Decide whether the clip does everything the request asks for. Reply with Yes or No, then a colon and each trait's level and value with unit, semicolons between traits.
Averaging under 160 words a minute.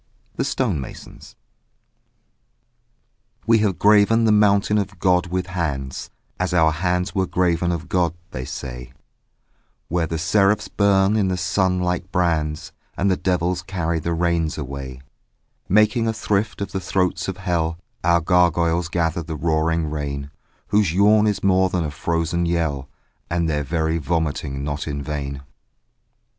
Yes: average, 150 wpm